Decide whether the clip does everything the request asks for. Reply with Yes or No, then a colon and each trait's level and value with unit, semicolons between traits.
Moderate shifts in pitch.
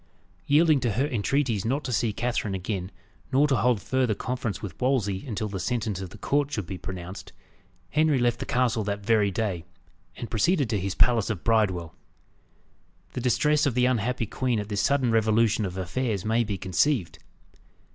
Yes: average, 4.2 semitones